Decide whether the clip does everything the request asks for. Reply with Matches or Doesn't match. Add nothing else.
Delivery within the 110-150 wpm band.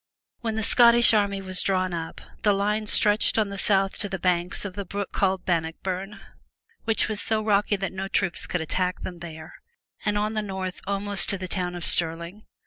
Doesn't match